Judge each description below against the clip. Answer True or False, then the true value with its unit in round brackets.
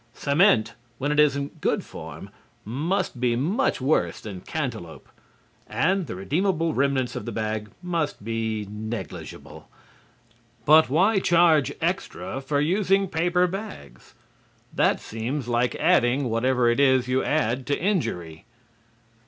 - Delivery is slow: True (130 wpm)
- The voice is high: False (140 Hz)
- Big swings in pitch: True (6.2 semitones)